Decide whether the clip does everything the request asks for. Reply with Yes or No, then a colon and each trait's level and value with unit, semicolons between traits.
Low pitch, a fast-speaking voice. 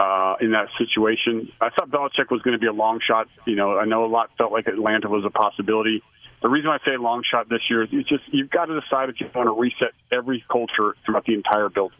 Yes: low, 115 Hz; fast, 265 wpm